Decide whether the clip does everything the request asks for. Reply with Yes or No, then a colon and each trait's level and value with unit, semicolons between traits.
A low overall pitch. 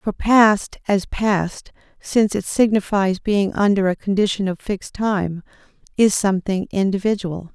No: high, 200 Hz